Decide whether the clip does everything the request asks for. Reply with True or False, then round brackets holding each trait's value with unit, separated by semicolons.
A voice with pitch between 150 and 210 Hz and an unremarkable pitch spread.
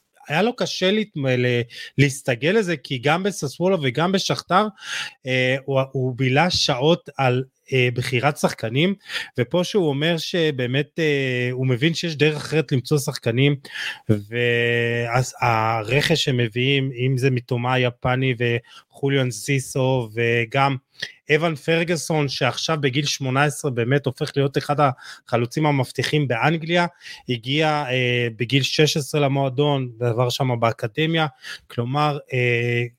False (140 Hz; 3.5 semitones)